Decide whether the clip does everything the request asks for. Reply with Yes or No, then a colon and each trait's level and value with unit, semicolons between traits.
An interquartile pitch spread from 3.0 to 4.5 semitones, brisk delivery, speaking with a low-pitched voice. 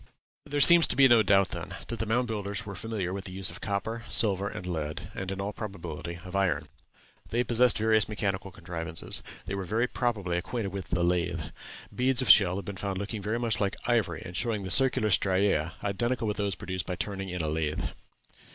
Yes: average, 3.6 semitones; fast, 210 wpm; low, 100 Hz